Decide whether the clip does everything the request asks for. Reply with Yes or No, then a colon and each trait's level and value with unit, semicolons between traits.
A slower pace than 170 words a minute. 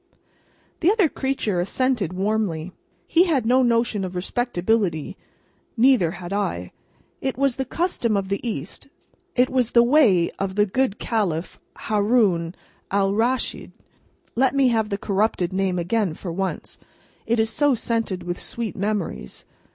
Yes: average, 145 wpm